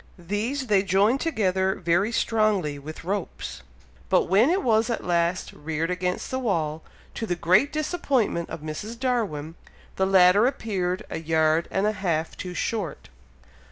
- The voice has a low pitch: No, high, 190 Hz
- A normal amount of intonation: Yes, average, 4.9 semitones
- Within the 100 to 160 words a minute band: Yes, average, 155 wpm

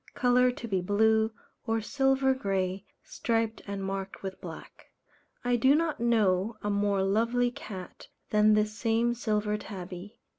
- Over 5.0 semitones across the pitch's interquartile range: No, average, 3.4 semitones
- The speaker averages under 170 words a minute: Yes, average, 150 wpm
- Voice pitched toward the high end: Yes, high, 215 Hz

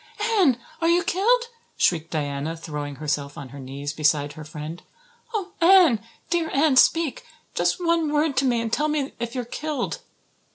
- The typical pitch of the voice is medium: No, high, 245 Hz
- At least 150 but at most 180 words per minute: Yes, average, 170 wpm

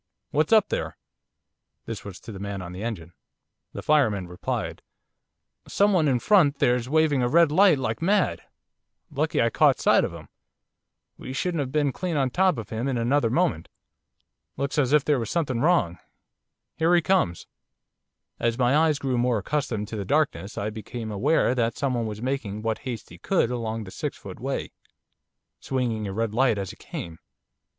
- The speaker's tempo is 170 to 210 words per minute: Yes, average, 180 wpm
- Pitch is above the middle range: No, low, 125 Hz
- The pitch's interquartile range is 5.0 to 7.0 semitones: Yes, wide, 5.6 semitones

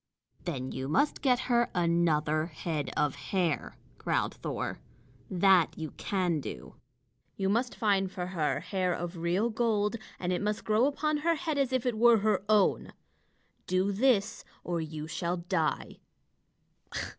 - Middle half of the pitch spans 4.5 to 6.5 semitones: Yes, average, 5.2 semitones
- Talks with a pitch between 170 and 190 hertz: Yes, medium, 185 Hz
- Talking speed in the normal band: Yes, average, 150 wpm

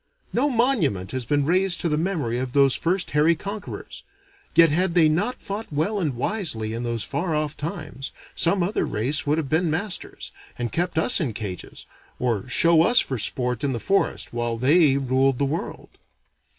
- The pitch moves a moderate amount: No, wide, 5.8 semitones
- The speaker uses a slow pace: No, average, 185 wpm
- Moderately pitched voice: Yes, medium, 155 Hz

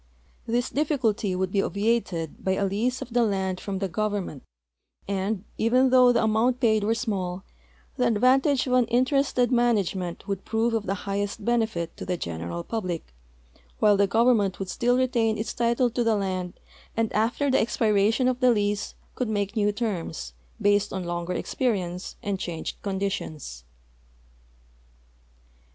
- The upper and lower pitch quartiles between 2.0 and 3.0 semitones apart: No, average, 3.9 semitones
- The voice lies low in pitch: No, high, 210 Hz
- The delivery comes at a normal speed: Yes, average, 160 wpm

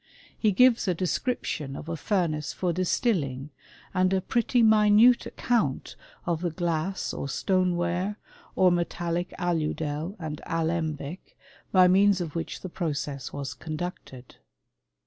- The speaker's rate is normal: No, slow, 130 wpm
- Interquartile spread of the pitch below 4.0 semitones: Yes, average, 3.6 semitones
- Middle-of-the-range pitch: Yes, medium, 175 Hz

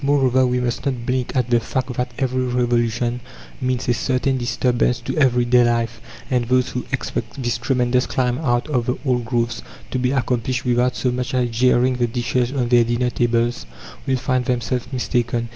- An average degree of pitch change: No, narrow, 1.1 semitones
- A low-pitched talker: Yes, low, 125 Hz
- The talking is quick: No, average, 185 wpm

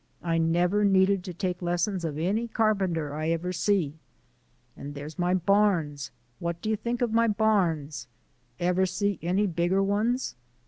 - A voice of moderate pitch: Yes, medium, 180 Hz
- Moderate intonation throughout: Yes, average, 3.7 semitones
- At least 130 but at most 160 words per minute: Yes, average, 155 wpm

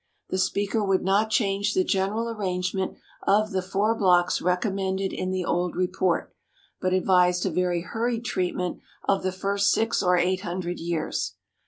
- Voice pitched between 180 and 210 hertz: Yes, high, 190 Hz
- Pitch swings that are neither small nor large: No, narrow, 1.8 semitones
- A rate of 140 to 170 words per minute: Yes, average, 160 wpm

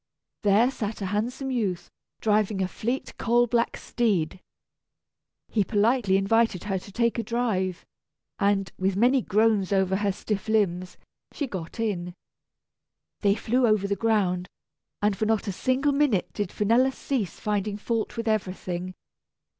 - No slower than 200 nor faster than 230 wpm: No, average, 145 wpm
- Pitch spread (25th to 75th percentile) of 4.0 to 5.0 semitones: No, average, 3.3 semitones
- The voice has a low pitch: No, high, 210 Hz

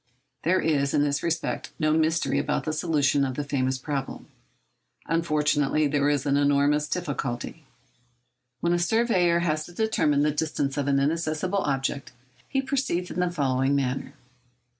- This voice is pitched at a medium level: Yes, medium, 150 Hz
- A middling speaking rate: Yes, average, 150 wpm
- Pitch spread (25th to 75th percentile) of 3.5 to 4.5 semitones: No, average, 3.1 semitones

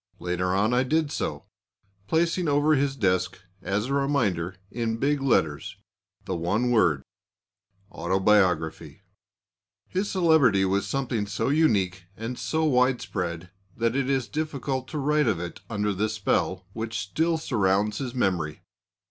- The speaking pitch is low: Yes, low, 115 Hz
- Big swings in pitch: Yes, wide, 6.6 semitones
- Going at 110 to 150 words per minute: Yes, average, 140 wpm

